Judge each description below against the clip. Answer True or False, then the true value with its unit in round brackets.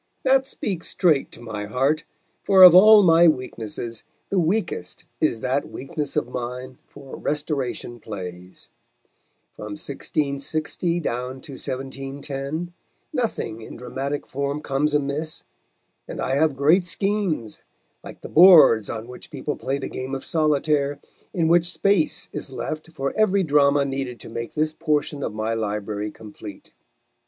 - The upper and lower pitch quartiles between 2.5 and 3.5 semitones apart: False (4.2 semitones)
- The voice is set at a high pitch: False (140 Hz)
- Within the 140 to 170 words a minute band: True (145 wpm)